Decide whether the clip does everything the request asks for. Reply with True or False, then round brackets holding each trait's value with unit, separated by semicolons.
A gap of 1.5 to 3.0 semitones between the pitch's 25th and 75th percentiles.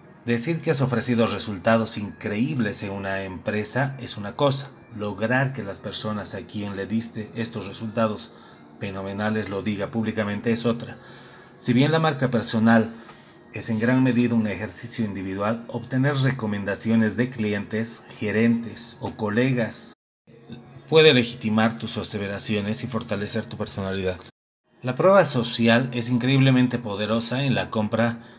True (2.4 semitones)